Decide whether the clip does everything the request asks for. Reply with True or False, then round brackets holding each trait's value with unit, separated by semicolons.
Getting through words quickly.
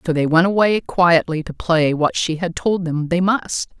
True (220 wpm)